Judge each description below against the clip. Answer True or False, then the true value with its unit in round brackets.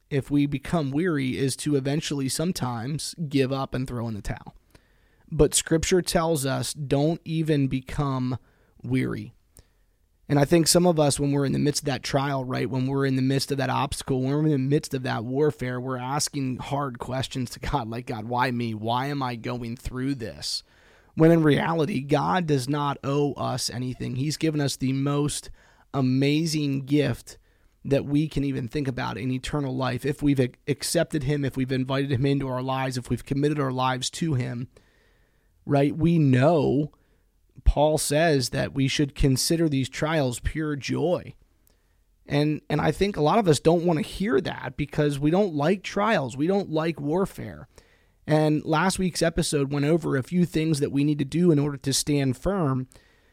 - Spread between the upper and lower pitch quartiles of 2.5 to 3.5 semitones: True (2.9 semitones)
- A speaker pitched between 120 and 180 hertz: True (140 Hz)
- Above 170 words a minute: True (190 wpm)